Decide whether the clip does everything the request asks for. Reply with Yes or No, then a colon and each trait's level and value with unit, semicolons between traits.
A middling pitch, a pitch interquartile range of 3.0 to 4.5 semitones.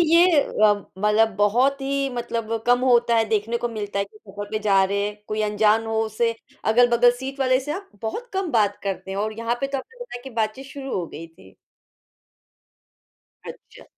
No: high, 225 Hz; average, 4.1 semitones